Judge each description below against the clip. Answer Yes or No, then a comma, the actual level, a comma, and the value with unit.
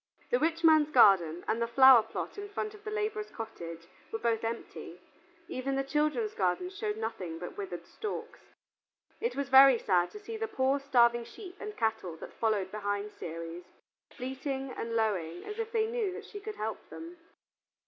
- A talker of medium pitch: No, very high, 260 Hz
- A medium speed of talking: Yes, average, 180 wpm